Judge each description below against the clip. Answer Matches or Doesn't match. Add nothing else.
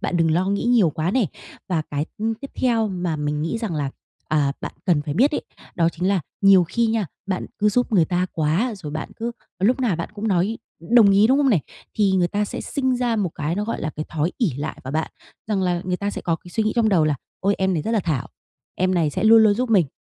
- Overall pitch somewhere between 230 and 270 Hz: Doesn't match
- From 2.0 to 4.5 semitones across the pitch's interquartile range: Doesn't match